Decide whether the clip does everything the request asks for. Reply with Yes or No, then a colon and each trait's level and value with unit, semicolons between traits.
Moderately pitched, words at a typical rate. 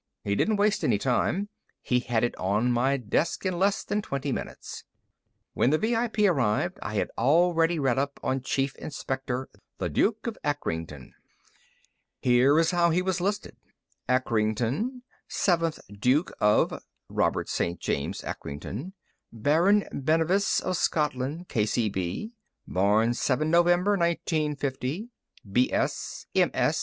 No: medium, 145 Hz; slow, 130 wpm